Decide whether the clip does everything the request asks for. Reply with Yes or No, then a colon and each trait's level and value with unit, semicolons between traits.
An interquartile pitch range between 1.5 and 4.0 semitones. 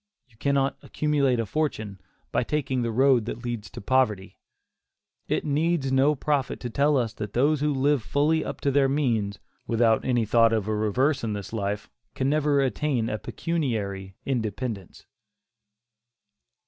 No: average, 4.6 semitones